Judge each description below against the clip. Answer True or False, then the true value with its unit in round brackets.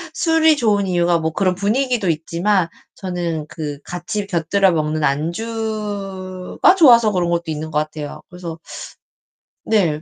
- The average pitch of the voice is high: False (180 Hz)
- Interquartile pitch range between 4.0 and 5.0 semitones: True (4.5 semitones)